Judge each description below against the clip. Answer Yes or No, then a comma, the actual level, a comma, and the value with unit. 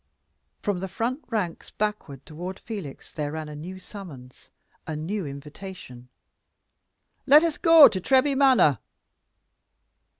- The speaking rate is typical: No, slow, 125 wpm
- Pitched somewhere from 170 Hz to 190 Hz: Yes, medium, 185 Hz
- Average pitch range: No, wide, 7.1 semitones